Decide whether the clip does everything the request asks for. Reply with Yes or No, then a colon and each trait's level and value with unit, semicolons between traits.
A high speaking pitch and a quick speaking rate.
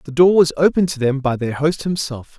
No: medium, 150 Hz; fast, 250 wpm